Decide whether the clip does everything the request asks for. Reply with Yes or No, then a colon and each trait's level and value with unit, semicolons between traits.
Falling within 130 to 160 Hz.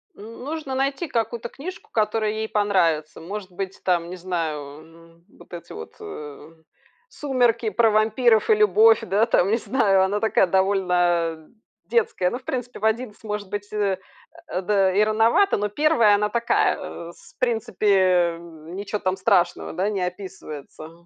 No: high, 205 Hz